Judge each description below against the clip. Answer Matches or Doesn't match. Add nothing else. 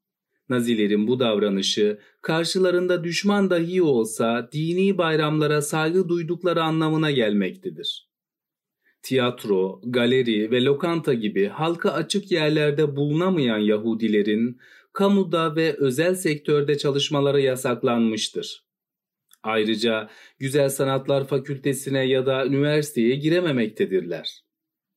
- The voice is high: Doesn't match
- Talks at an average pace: Doesn't match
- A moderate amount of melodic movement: Doesn't match